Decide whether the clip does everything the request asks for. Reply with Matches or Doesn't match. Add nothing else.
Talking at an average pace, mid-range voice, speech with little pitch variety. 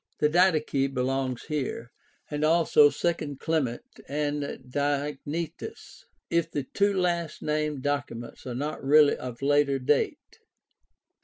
Doesn't match